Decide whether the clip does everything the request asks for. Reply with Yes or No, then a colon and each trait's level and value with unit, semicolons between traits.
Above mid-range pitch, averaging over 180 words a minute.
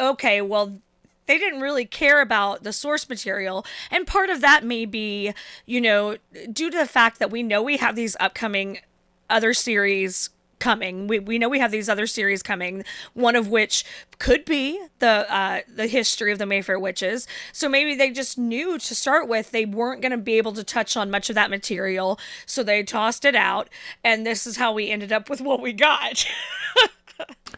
Yes: high, 225 Hz; average, 200 wpm